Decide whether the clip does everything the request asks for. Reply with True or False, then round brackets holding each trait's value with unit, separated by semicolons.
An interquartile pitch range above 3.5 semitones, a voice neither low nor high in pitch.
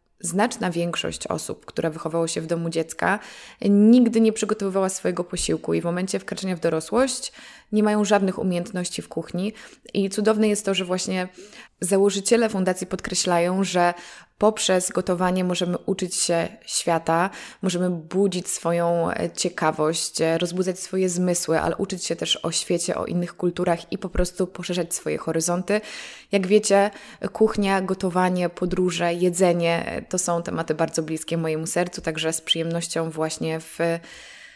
False (2.7 semitones; 180 Hz)